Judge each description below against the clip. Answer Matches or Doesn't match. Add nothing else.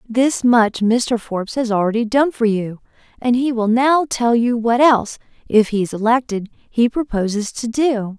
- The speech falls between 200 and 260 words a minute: Doesn't match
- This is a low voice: Doesn't match